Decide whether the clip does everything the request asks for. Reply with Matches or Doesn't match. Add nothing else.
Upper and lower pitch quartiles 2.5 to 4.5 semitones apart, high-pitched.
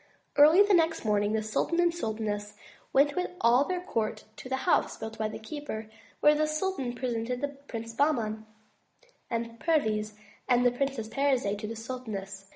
Doesn't match